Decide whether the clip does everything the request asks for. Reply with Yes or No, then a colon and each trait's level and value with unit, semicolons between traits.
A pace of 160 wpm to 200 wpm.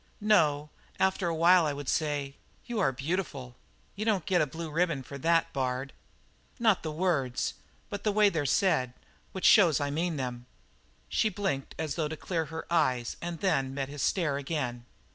Yes: average, 185 wpm